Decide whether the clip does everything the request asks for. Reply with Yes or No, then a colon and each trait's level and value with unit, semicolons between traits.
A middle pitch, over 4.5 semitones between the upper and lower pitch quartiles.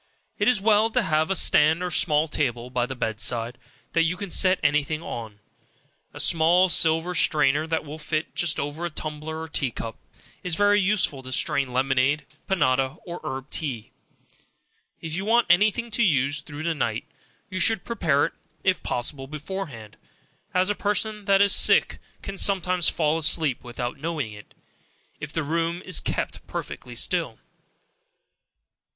Yes: medium, 160 Hz; average, 5.2 semitones